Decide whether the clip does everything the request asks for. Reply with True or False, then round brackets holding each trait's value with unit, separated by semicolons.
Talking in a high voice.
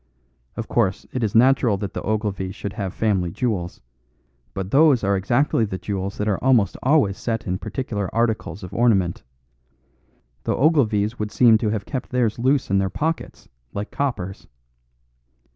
False (110 Hz)